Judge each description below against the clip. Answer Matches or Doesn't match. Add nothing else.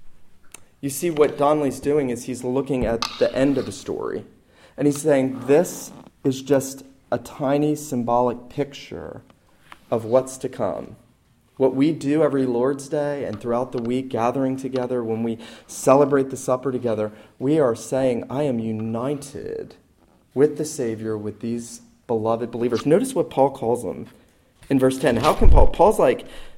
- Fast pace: Doesn't match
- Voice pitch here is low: Matches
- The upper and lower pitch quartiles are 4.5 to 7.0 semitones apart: Doesn't match